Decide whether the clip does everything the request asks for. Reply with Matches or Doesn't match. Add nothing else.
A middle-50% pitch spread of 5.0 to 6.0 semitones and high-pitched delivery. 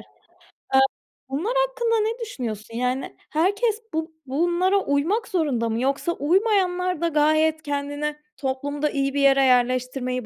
Matches